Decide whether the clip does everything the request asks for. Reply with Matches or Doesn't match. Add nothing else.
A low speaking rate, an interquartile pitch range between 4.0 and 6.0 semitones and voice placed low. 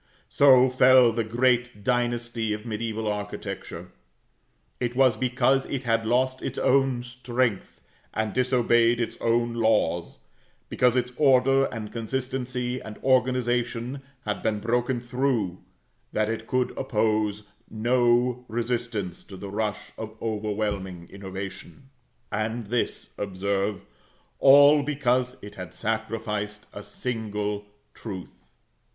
Doesn't match